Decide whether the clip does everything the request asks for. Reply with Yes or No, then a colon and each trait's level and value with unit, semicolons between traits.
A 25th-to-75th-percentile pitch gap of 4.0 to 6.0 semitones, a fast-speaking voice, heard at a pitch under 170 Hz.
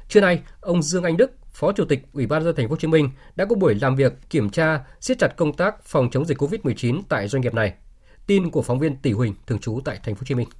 Yes: average, 4.7 semitones; fast, 285 wpm; medium, 140 Hz